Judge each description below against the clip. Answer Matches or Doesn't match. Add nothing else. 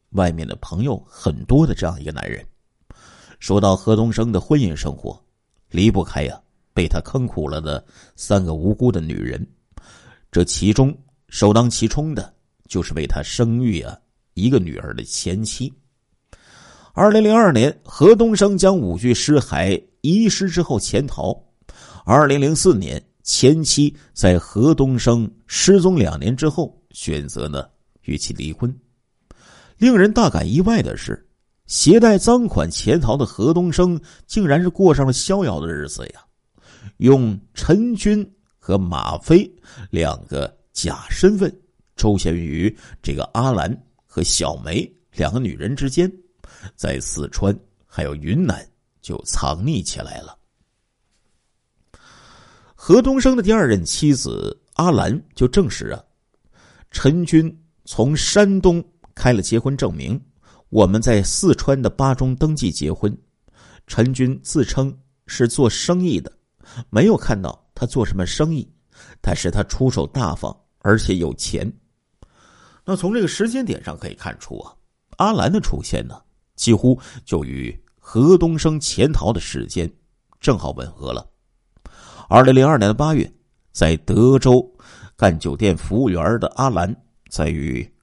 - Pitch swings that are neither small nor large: Doesn't match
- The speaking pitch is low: Matches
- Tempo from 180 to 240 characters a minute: Matches